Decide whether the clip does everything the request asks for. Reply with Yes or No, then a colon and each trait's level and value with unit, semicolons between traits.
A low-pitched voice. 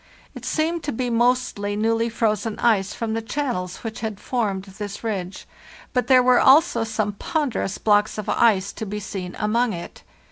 No: high, 220 Hz